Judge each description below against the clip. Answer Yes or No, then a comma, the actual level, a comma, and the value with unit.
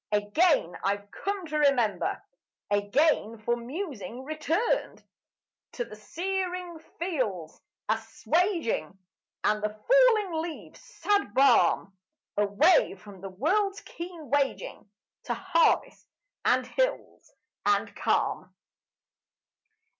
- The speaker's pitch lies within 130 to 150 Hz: No, very high, 285 Hz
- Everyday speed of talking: No, slow, 95 wpm